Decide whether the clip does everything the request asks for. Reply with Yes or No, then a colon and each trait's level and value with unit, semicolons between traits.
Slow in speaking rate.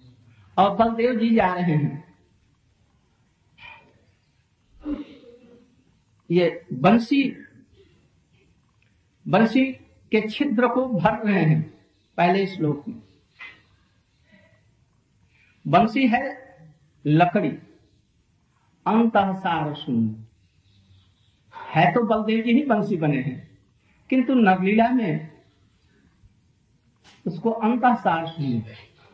Yes: slow, 80 wpm